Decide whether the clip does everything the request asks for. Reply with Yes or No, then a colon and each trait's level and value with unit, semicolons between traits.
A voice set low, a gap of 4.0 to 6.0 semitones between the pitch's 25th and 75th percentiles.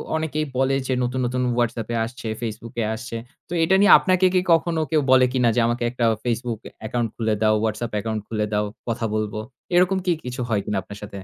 No: low, 120 Hz; average, 3.1 semitones